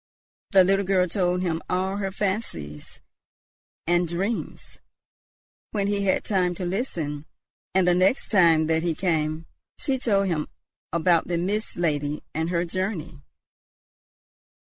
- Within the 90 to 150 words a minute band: Yes, slow, 135 wpm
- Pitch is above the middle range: No, medium, 180 Hz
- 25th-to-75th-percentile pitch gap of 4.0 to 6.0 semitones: No, average, 3.2 semitones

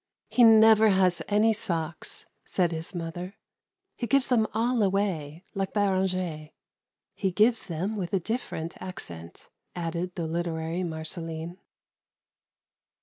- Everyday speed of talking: No, slow, 120 wpm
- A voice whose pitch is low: No, medium, 185 Hz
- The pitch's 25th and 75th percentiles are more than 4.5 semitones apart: No, average, 4.2 semitones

